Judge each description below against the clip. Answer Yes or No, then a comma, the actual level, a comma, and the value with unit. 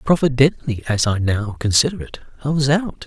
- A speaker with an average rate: Yes, average, 175 wpm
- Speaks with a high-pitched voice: No, low, 130 Hz